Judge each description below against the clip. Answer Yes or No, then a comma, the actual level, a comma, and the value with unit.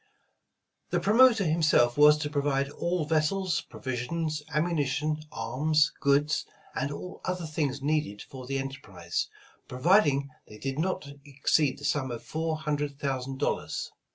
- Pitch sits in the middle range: Yes, medium, 145 Hz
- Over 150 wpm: No, average, 145 wpm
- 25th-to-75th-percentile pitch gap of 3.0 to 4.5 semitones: No, narrow, 2.6 semitones